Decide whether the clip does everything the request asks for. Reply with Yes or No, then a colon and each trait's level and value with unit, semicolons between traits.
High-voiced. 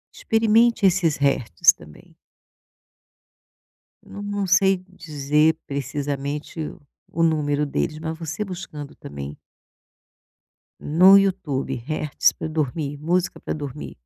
No: medium, 155 Hz